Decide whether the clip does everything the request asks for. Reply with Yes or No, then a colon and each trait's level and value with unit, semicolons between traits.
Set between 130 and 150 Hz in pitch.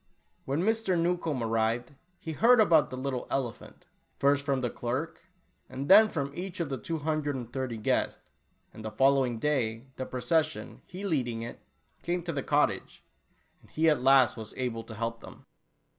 Yes: low, 135 Hz